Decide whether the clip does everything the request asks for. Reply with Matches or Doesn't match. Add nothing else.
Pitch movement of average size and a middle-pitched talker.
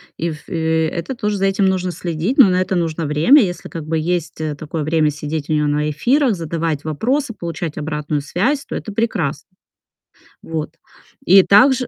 Matches